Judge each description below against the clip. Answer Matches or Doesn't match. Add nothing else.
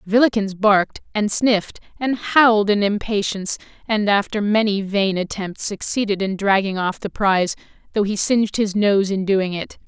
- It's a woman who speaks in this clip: Matches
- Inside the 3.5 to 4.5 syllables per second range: Doesn't match